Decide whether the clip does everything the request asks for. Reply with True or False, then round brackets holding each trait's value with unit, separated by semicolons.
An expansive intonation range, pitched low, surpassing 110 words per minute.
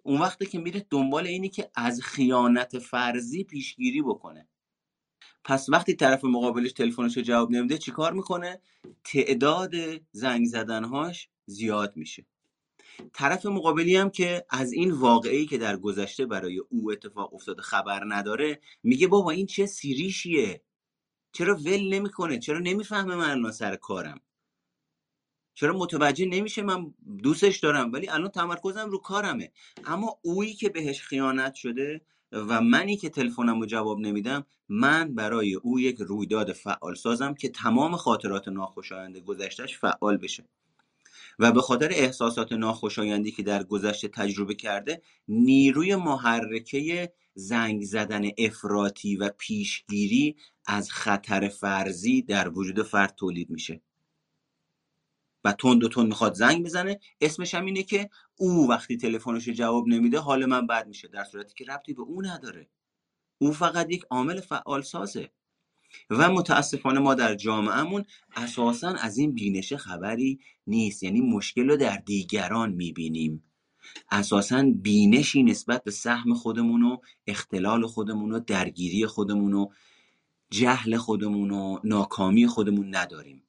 True (8.6 semitones; 125 Hz; 135 wpm)